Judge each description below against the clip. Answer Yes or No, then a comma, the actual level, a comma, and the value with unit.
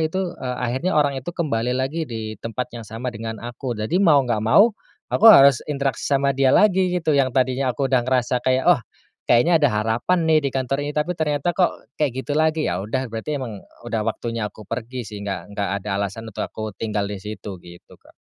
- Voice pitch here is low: Yes, low, 130 Hz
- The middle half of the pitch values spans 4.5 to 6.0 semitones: Yes, average, 4.8 semitones